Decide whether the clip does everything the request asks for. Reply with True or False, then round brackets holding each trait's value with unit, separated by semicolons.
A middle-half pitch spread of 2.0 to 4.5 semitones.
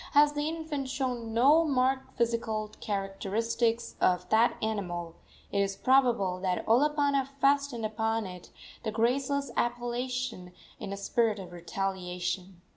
False (5.2 semitones)